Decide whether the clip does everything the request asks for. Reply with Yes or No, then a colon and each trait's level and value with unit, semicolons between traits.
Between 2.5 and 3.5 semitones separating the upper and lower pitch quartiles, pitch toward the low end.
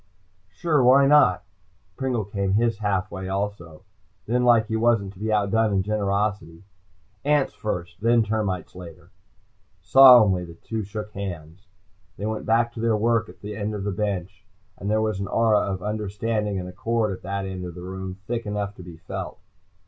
Yes: average, 2.8 semitones; low, 105 Hz